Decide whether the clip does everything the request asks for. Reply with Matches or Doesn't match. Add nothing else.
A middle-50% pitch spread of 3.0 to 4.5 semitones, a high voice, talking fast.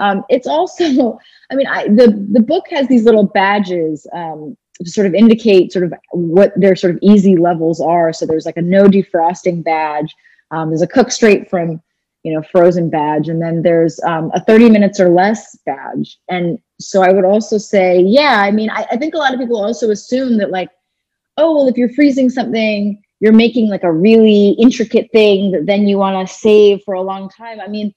Matches